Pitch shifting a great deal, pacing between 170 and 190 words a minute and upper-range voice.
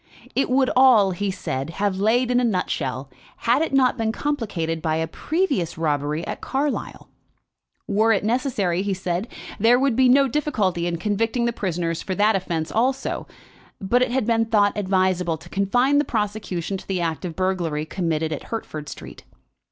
Yes: wide, 6.1 semitones; average, 175 wpm; high, 200 Hz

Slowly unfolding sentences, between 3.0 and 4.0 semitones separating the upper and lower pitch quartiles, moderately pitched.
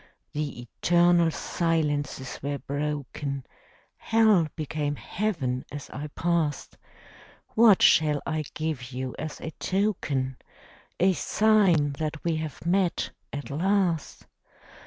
Yes: slow, 110 wpm; average, 3.5 semitones; medium, 155 Hz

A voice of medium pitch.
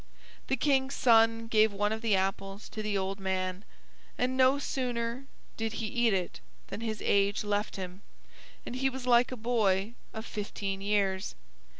No: high, 220 Hz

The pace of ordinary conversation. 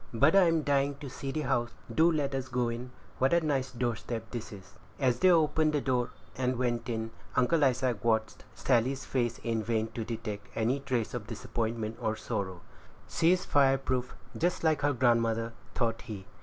Yes: average, 185 wpm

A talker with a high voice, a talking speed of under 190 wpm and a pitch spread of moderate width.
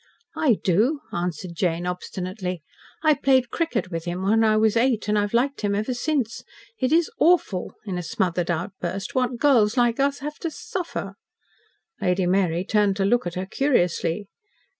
No: high, 210 Hz; average, 170 wpm; wide, 6.1 semitones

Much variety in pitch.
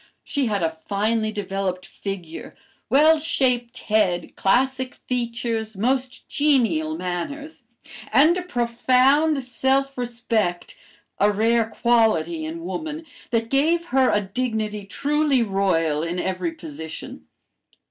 Yes: wide, 5.7 semitones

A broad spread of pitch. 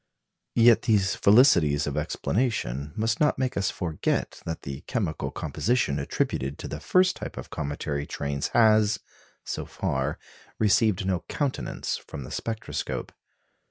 Yes: wide, 7.9 semitones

